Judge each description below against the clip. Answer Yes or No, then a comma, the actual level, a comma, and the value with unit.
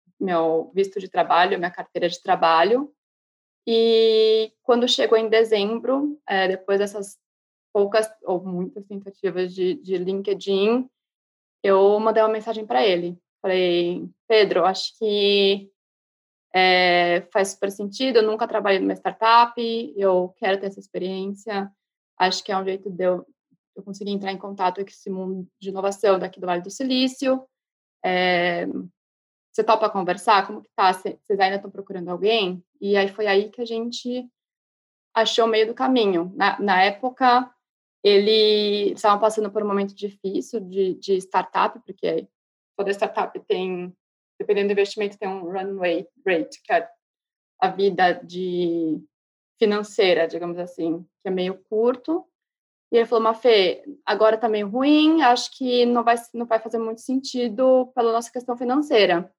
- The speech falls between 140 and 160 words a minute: Yes, average, 155 wpm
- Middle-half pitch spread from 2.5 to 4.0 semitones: Yes, average, 3.7 semitones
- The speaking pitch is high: Yes, high, 205 Hz